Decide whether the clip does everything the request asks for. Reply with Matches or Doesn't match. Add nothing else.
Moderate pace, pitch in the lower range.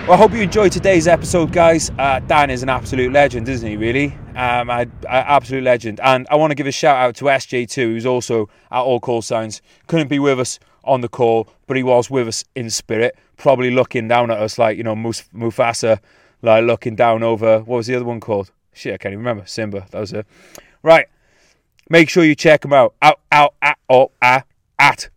Doesn't match